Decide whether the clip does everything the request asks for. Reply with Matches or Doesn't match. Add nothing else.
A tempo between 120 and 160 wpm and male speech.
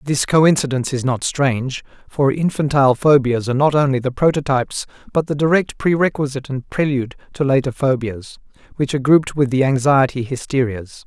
Matches